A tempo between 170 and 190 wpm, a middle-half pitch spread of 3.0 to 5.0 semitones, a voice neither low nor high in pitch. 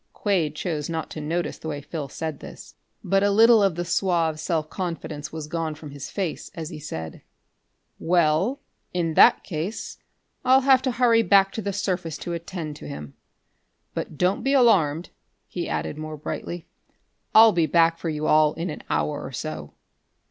Yes: average, 180 wpm; average, 4.2 semitones; medium, 165 Hz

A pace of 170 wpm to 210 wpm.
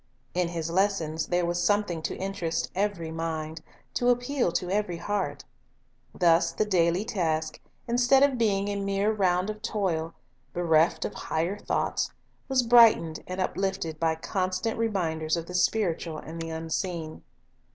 No: average, 150 wpm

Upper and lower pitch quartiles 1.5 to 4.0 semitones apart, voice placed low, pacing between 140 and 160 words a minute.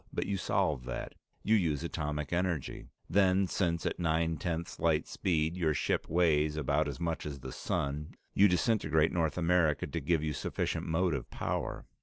No: average, 2.8 semitones; very low, 80 Hz; average, 170 wpm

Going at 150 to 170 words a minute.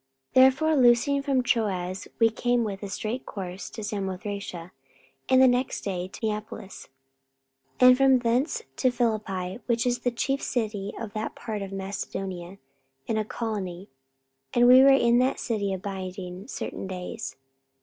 Yes: average, 160 wpm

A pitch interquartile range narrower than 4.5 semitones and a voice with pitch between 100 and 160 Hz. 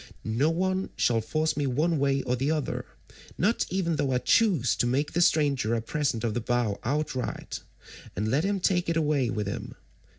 No: average, 5.2 semitones; medium, 140 Hz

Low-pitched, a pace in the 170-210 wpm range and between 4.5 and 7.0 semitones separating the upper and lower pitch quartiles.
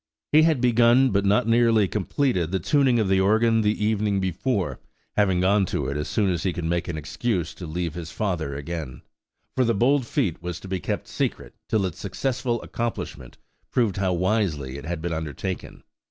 Yes: very low, 95 Hz; average, 195 wpm; average, 5.2 semitones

